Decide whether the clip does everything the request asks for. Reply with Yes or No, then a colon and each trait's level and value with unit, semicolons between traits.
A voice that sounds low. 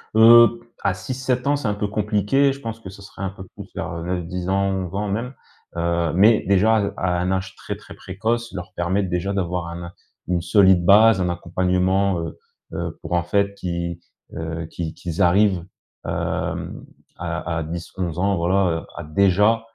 Yes: very low, 95 Hz